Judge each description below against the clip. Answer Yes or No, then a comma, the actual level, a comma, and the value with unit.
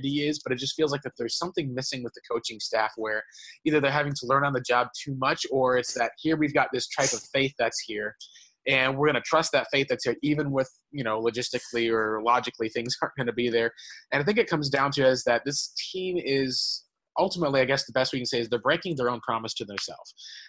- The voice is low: Yes, low, 130 Hz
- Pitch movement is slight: No, average, 3.3 semitones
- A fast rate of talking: Yes, fast, 250 wpm